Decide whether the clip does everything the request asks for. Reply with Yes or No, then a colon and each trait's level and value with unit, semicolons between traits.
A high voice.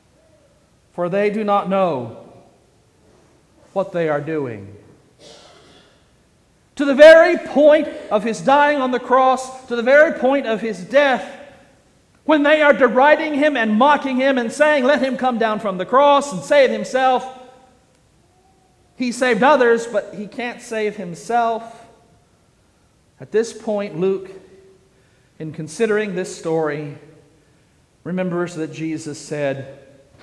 Yes: high, 220 Hz